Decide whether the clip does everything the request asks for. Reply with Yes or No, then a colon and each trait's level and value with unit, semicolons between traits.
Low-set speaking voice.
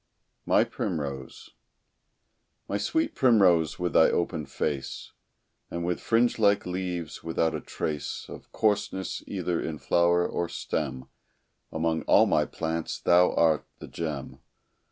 Yes: very low, 85 Hz